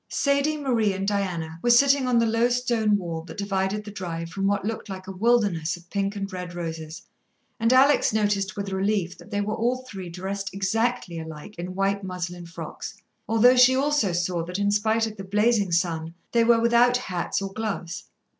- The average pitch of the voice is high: Yes, high, 200 Hz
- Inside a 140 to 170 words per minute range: No, average, 195 wpm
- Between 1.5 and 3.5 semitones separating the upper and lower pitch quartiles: No, average, 4.1 semitones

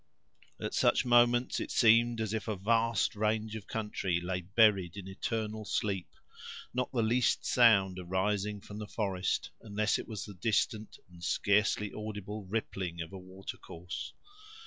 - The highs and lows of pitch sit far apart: No, average, 2.7 semitones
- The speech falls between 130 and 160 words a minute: Yes, average, 155 wpm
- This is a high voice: No, low, 105 Hz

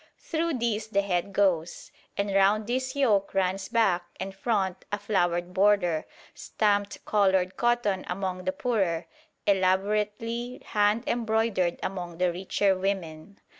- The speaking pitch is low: No, high, 195 Hz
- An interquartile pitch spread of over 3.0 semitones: No, average, 2.7 semitones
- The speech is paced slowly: Yes, slow, 130 wpm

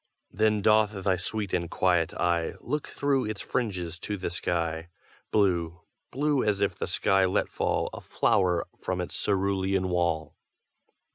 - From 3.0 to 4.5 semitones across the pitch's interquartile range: Yes, average, 3.4 semitones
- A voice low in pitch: Yes, very low, 95 Hz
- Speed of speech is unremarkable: Yes, average, 150 wpm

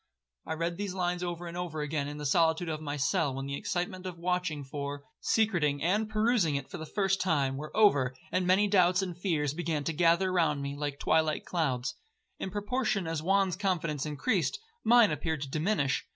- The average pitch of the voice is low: No, medium, 170 Hz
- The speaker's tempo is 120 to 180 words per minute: No, average, 195 wpm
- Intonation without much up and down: No, average, 4.0 semitones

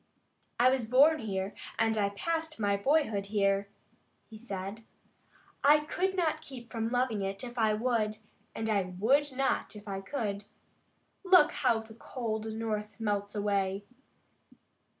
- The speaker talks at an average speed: Yes, average, 145 wpm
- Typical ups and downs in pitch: Yes, average, 4.3 semitones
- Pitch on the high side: Yes, high, 220 Hz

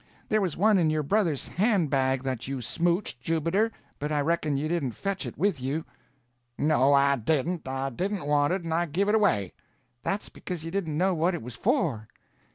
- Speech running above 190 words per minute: Yes, average, 200 wpm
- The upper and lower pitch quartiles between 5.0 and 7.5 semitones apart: Yes, wide, 5.4 semitones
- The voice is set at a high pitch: No, medium, 160 Hz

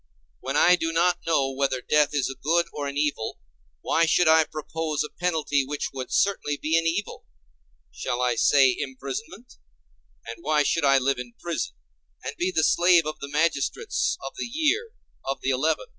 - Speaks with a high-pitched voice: No, medium, 150 Hz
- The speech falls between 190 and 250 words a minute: No, average, 180 wpm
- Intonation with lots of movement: No, average, 3.5 semitones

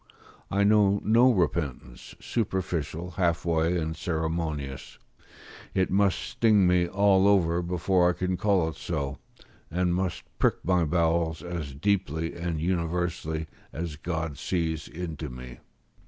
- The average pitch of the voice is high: No, very low, 85 Hz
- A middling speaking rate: No, slow, 130 wpm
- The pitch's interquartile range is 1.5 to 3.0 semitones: Yes, narrow, 2.6 semitones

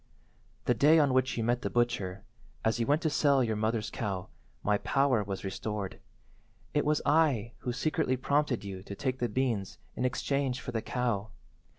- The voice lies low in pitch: Yes, low, 120 Hz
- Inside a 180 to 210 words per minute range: Yes, average, 185 wpm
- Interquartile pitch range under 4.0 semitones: No, average, 4.5 semitones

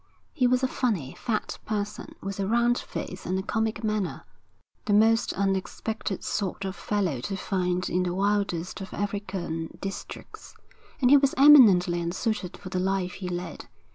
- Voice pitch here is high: Yes, high, 195 Hz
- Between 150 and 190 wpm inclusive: Yes, average, 165 wpm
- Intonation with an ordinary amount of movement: Yes, average, 3.2 semitones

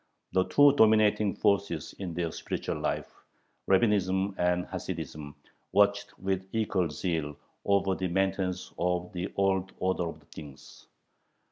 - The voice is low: Yes, very low, 95 Hz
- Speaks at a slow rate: Yes, slow, 125 wpm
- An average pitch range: No, narrow, 2.2 semitones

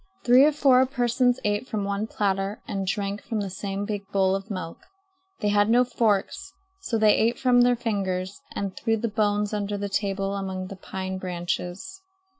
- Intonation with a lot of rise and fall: No, average, 3.1 semitones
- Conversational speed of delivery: Yes, average, 185 wpm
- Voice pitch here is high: Yes, high, 205 Hz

